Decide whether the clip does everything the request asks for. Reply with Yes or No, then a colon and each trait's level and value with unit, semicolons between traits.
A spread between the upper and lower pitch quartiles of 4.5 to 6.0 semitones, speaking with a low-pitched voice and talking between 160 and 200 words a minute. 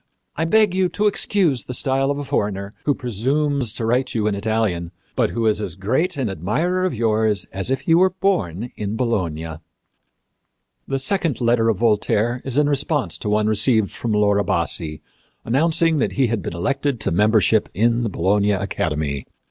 Yes: wide, 5.6 semitones; low, 115 Hz; average, 180 wpm